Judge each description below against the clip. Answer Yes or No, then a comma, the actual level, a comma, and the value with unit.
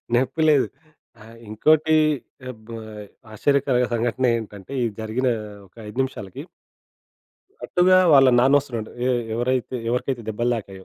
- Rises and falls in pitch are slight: No, average, 3.4 semitones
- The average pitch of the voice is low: Yes, low, 120 Hz